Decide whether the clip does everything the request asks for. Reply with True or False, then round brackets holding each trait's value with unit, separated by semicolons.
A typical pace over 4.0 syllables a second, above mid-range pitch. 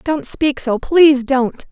False (3.7 syllables/s; 270 Hz)